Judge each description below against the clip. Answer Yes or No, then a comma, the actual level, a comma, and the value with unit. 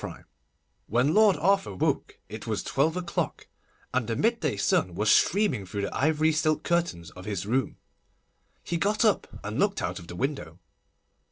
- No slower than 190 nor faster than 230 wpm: No, average, 175 wpm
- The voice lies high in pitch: No, medium, 150 Hz